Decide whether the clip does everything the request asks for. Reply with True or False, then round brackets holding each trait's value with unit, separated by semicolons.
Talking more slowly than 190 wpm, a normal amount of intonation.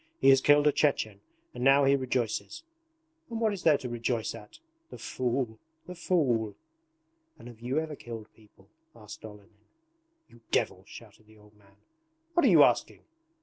True (170 wpm; 4.9 semitones)